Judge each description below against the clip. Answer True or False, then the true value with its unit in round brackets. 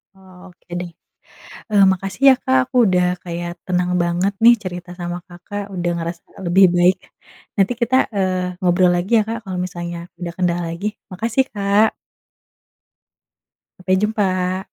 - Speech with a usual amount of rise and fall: False (2.1 semitones)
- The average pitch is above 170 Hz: True (185 Hz)